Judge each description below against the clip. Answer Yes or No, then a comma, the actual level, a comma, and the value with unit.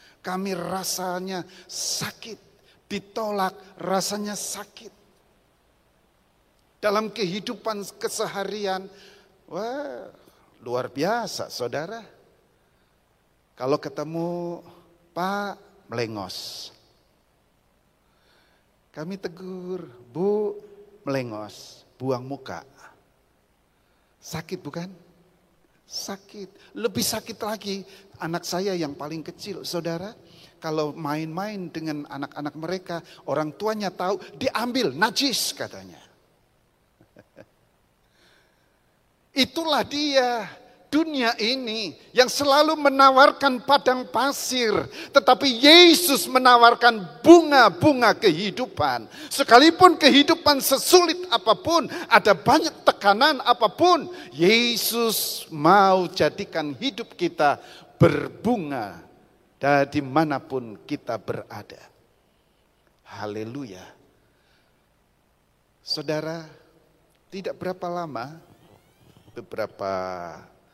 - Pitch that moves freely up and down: Yes, wide, 6.8 semitones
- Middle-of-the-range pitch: No, high, 195 Hz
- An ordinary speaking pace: No, slow, 70 wpm